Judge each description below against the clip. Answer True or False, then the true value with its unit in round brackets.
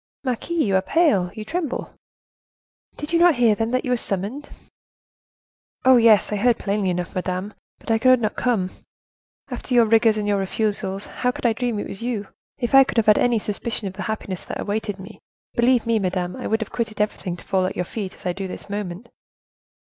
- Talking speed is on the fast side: True (215 wpm)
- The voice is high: True (215 Hz)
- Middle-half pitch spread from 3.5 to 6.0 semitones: True (3.8 semitones)